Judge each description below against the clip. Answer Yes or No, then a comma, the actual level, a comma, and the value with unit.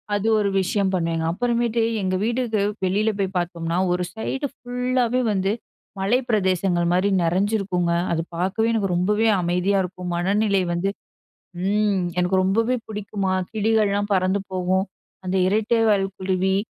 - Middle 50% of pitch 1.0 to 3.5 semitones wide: Yes, average, 2.9 semitones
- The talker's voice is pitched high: Yes, high, 195 Hz